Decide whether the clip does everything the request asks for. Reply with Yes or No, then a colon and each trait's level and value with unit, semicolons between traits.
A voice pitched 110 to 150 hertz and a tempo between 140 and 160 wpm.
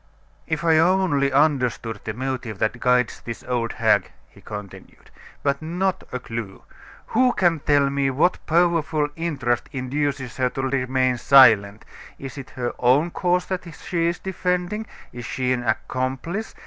Yes: medium, 140 Hz; average, 150 wpm